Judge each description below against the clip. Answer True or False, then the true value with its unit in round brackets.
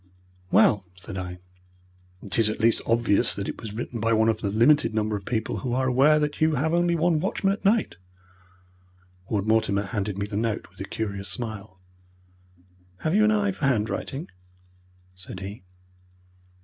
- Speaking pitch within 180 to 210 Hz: False (115 Hz)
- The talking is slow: False (175 wpm)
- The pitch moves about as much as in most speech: False (6.6 semitones)